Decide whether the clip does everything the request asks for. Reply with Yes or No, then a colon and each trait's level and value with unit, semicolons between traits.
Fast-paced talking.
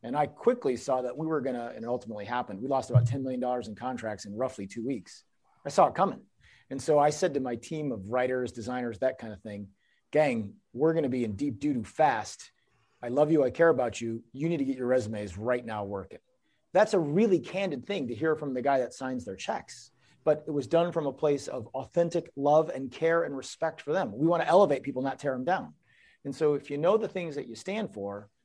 Yes: fast, 245 wpm